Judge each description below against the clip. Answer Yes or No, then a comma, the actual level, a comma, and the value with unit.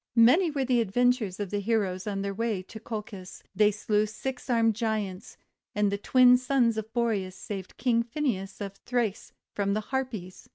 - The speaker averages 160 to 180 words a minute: Yes, average, 175 wpm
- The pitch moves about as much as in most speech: Yes, average, 3.5 semitones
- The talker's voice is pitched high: Yes, high, 220 Hz